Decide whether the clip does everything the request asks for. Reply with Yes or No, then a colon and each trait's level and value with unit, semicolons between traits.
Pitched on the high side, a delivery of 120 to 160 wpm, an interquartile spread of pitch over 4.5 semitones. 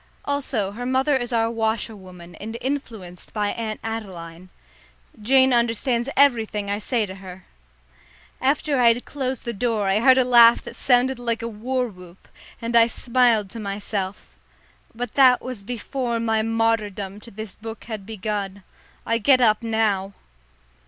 No: high, 225 Hz; average, 155 wpm; average, 3.2 semitones